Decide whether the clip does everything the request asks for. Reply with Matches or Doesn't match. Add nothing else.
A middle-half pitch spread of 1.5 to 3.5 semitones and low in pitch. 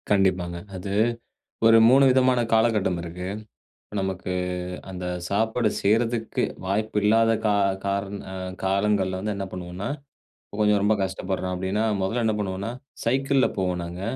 Matches